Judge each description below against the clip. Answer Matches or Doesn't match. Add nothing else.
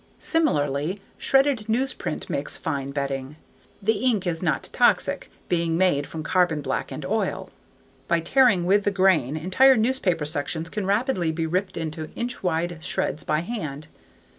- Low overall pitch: Doesn't match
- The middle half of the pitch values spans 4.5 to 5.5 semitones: Matches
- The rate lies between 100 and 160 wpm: Matches